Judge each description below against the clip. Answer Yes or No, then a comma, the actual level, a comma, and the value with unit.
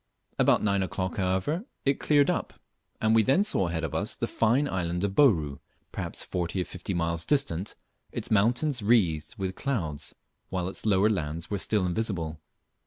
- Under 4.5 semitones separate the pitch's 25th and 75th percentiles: No, average, 5.0 semitones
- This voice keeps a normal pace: Yes, average, 175 wpm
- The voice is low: Yes, very low, 95 Hz